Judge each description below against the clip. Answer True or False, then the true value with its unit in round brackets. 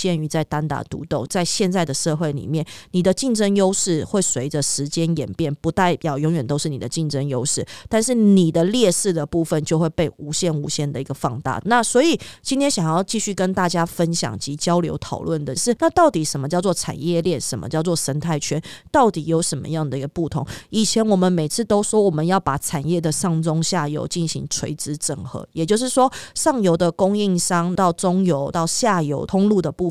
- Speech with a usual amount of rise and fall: True (3.8 semitones)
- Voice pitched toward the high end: False (165 Hz)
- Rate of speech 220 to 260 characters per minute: False (315 characters per minute)